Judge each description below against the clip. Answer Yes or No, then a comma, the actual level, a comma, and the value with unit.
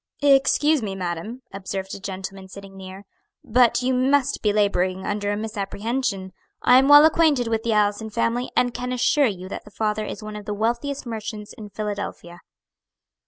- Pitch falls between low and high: No, high, 215 Hz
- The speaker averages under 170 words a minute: No, average, 175 wpm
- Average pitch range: Yes, average, 4.1 semitones